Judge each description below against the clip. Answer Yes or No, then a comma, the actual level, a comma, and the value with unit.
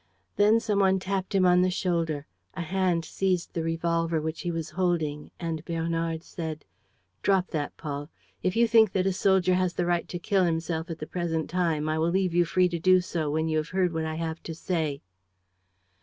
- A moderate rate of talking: No, fast, 210 wpm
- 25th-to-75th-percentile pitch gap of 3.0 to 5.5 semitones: No, narrow, 2.4 semitones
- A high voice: No, medium, 170 Hz